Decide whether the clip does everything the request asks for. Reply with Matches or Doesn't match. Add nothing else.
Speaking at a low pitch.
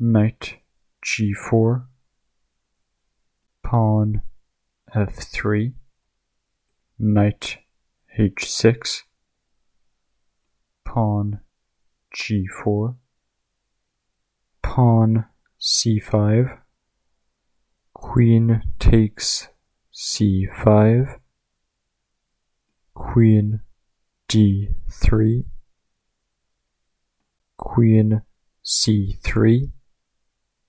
Matches